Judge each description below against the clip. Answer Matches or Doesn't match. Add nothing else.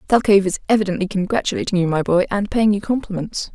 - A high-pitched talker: Matches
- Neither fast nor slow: Matches